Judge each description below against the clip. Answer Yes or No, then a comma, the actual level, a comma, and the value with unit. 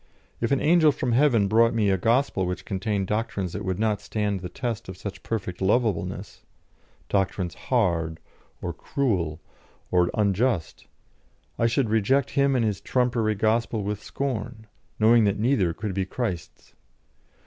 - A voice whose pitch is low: Yes, low, 105 Hz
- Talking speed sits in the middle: Yes, average, 150 wpm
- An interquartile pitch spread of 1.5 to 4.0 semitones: Yes, average, 3.7 semitones